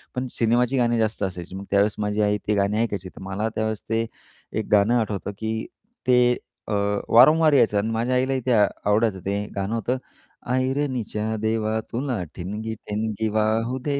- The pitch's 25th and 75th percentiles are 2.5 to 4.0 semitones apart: Yes, average, 2.8 semitones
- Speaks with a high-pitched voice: No, low, 110 Hz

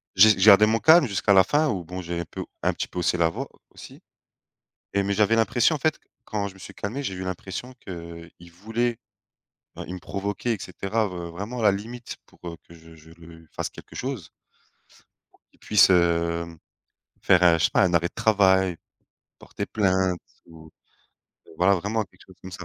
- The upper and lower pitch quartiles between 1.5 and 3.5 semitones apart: No, average, 3.9 semitones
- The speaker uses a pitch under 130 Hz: Yes, very low, 95 Hz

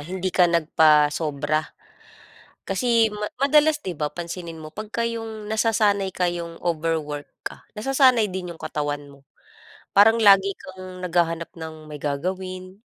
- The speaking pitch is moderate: Yes, medium, 180 Hz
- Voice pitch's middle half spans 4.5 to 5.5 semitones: Yes, average, 4.9 semitones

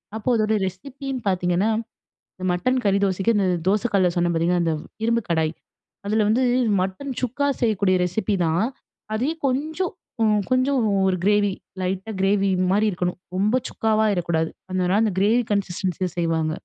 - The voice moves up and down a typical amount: Yes, average, 3.8 semitones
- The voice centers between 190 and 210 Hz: Yes, high, 200 Hz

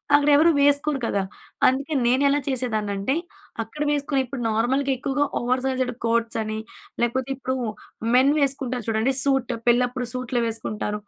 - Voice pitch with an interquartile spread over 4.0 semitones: No, average, 2.9 semitones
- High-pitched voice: Yes, very high, 255 Hz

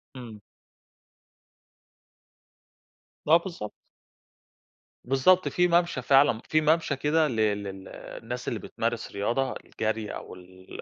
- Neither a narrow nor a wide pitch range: No, wide, 6.7 semitones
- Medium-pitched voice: No, low, 125 Hz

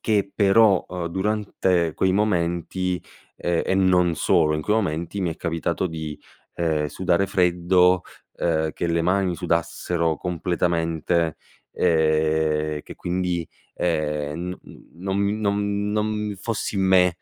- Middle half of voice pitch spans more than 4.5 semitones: No, narrow, 2.6 semitones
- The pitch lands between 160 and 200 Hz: No, very low, 90 Hz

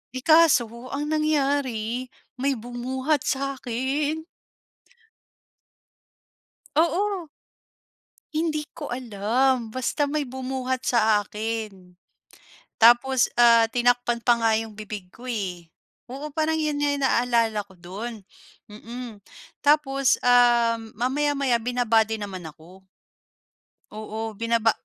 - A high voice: Yes, high, 245 Hz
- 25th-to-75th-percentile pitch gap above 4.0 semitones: No, average, 3.7 semitones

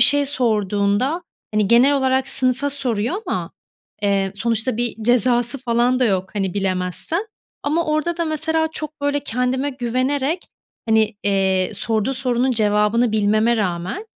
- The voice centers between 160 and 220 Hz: No, high, 240 Hz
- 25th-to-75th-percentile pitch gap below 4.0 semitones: No, average, 5.1 semitones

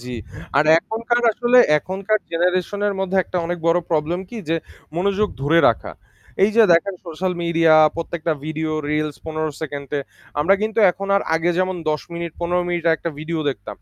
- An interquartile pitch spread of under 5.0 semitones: Yes, average, 3.5 semitones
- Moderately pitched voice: Yes, medium, 170 Hz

